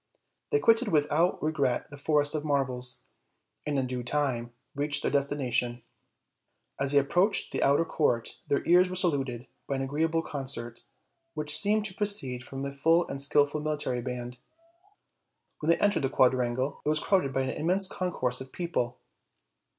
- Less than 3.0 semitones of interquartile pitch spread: No, average, 4.1 semitones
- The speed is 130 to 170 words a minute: Yes, average, 165 wpm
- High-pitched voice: No, medium, 145 Hz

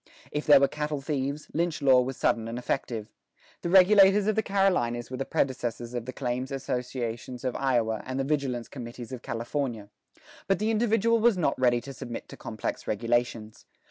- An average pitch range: Yes, average, 4.2 semitones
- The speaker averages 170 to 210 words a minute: Yes, average, 180 wpm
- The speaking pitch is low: Yes, low, 130 Hz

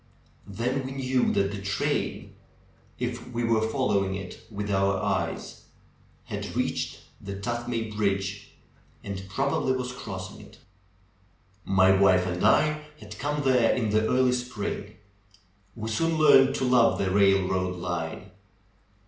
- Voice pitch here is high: No, low, 105 Hz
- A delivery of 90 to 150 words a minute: Yes, average, 140 wpm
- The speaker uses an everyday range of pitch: Yes, average, 4.6 semitones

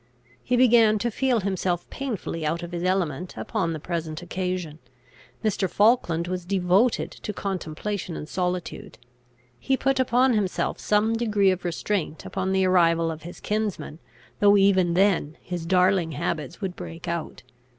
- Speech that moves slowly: No, average, 150 wpm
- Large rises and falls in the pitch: No, average, 3.6 semitones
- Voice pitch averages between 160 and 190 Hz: Yes, medium, 185 Hz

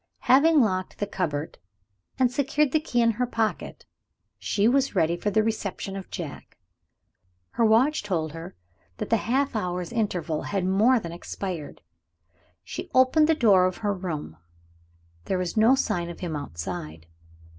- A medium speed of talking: Yes, average, 155 wpm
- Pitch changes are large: Yes, wide, 5.9 semitones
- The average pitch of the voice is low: No, high, 205 Hz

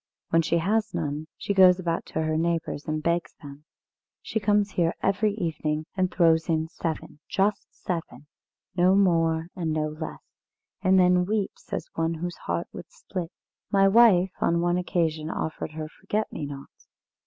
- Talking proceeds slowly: No, average, 165 wpm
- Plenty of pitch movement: No, average, 3.2 semitones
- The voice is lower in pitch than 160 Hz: No, medium, 170 Hz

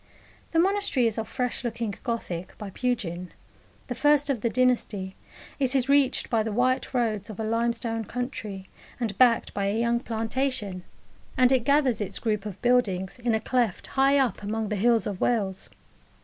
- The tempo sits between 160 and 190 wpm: Yes, average, 175 wpm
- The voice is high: Yes, high, 230 Hz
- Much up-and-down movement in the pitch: No, average, 3.3 semitones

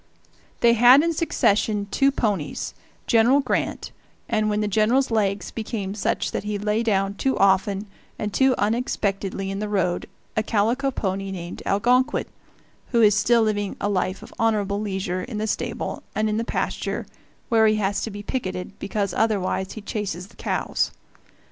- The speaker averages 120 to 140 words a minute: No, average, 165 wpm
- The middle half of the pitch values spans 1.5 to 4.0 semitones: Yes, narrow, 2.6 semitones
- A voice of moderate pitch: No, high, 210 Hz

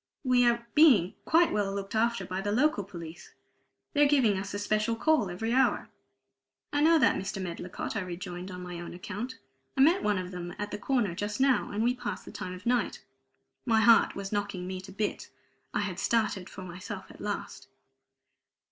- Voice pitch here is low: No, high, 205 Hz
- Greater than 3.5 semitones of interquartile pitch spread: Yes, average, 4.5 semitones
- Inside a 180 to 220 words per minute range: Yes, average, 195 wpm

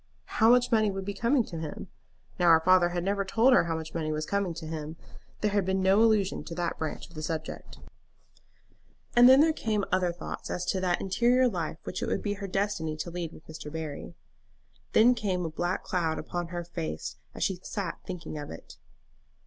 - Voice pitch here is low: No, medium, 180 Hz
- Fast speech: Yes, fast, 215 wpm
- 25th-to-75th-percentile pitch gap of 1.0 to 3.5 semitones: No, average, 4.0 semitones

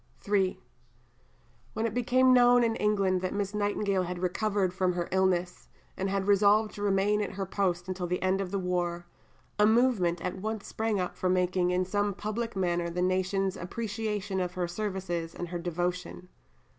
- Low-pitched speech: No, high, 190 Hz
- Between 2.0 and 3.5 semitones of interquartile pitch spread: Yes, narrow, 2.6 semitones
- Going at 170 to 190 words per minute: Yes, average, 180 wpm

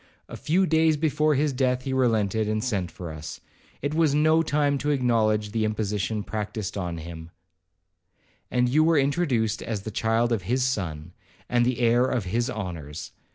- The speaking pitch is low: Yes, low, 120 Hz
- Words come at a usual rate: Yes, average, 175 wpm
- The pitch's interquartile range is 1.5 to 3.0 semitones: No, average, 5.2 semitones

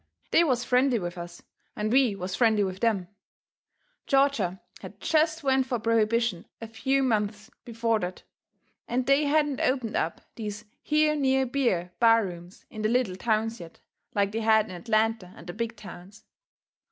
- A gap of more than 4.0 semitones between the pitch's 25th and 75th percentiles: Yes, average, 4.4 semitones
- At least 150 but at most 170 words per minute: Yes, average, 165 wpm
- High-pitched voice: Yes, high, 225 Hz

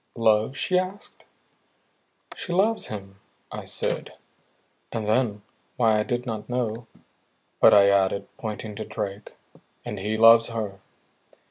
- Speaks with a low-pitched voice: Yes, low, 110 Hz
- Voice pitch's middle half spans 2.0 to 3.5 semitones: Yes, average, 2.8 semitones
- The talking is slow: Yes, slow, 130 wpm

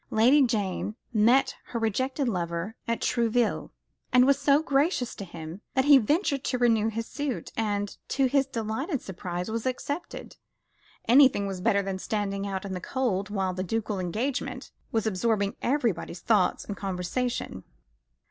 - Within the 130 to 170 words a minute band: Yes, average, 155 wpm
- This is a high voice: Yes, high, 225 Hz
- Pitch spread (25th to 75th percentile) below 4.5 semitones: No, average, 4.8 semitones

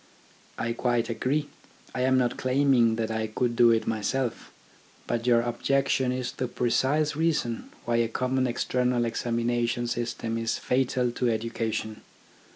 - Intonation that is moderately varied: No, narrow, 1.7 semitones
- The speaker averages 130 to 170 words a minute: Yes, average, 145 wpm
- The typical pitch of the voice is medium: No, low, 120 Hz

